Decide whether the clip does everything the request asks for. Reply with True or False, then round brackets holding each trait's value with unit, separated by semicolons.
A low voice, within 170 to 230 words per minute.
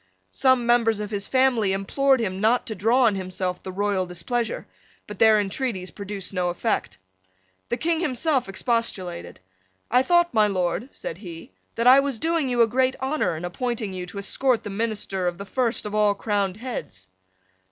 False (215 Hz; 180 wpm)